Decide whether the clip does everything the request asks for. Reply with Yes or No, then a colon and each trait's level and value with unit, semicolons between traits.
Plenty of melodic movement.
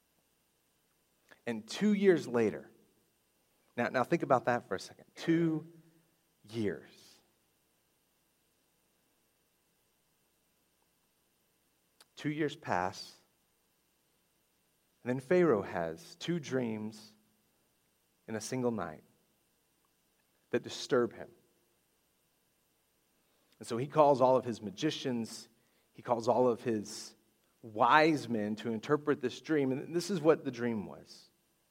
Yes: wide, 5.7 semitones